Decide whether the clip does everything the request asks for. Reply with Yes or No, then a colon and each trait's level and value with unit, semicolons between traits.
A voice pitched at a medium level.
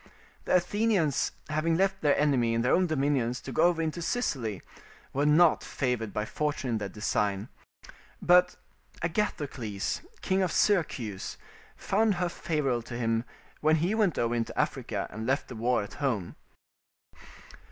Yes: medium, 145 Hz